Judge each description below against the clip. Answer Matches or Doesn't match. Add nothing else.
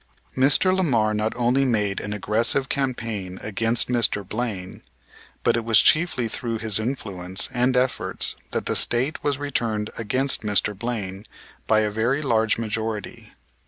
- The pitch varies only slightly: Doesn't match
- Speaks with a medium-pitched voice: Doesn't match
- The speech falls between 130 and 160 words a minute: Matches